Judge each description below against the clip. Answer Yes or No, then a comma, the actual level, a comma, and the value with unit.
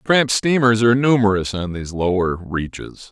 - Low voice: Yes, low, 110 Hz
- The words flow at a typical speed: Yes, average, 155 wpm